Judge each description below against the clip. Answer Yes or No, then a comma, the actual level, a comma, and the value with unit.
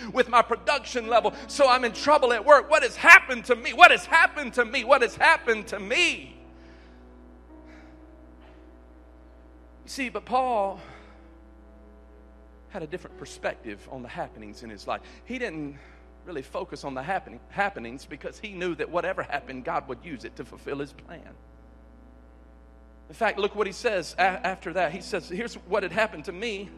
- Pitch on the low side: No, high, 195 Hz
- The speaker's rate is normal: Yes, average, 170 wpm